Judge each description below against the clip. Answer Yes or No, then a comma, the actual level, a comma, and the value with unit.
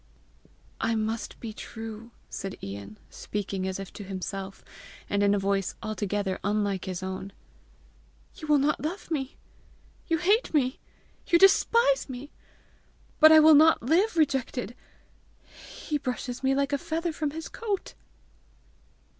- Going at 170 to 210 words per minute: No, average, 140 wpm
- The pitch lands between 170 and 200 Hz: No, high, 245 Hz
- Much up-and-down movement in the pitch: Yes, wide, 7.6 semitones